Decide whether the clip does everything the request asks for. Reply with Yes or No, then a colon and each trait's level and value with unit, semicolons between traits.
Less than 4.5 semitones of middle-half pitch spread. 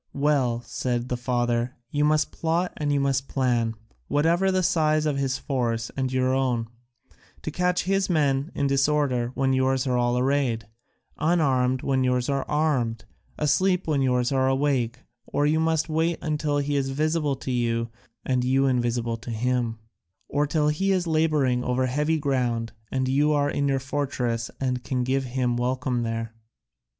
Yes: average, 3.2 semitones